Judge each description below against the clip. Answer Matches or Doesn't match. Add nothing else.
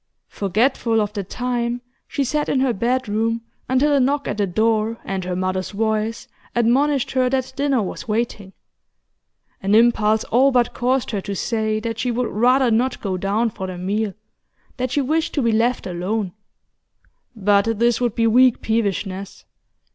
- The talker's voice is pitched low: Doesn't match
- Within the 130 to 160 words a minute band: Doesn't match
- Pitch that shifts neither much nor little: Matches